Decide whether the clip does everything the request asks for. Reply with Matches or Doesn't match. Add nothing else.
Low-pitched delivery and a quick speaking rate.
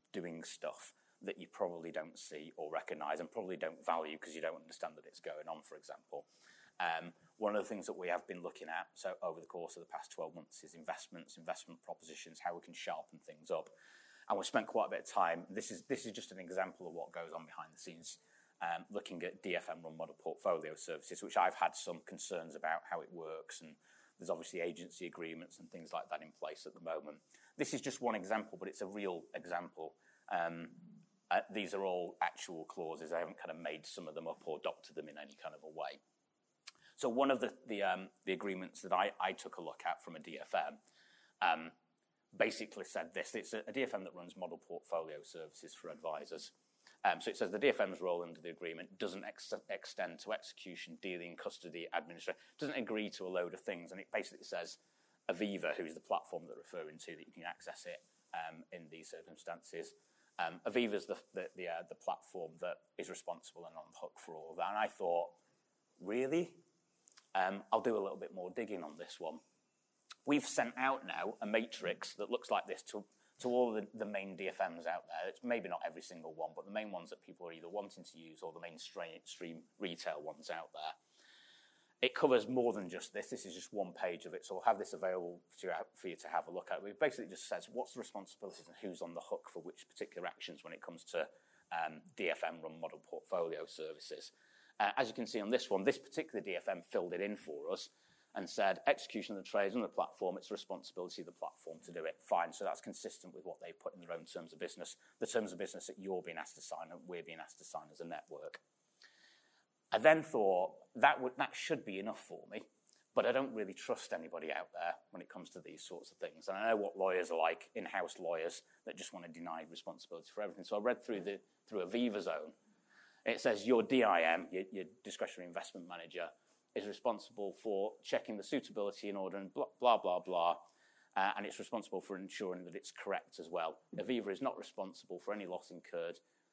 Matches